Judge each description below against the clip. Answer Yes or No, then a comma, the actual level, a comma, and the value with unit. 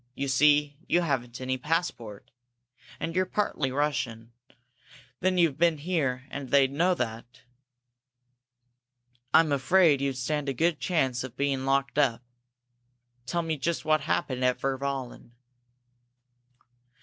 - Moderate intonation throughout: Yes, average, 3.7 semitones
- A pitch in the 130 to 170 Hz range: Yes, medium, 140 Hz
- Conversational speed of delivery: No, slow, 125 wpm